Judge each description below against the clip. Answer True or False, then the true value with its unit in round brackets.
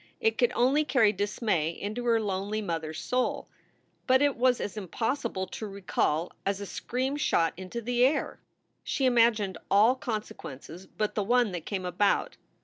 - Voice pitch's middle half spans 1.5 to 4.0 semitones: False (4.6 semitones)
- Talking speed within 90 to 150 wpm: False (165 wpm)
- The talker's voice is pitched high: True (215 Hz)